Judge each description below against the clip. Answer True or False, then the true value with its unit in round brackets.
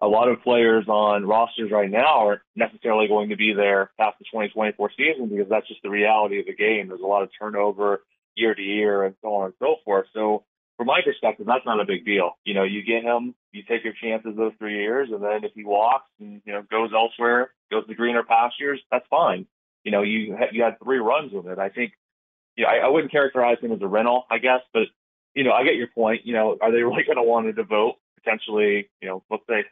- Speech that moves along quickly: True (250 wpm)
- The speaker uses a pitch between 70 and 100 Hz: False (110 Hz)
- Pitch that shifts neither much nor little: False (2.0 semitones)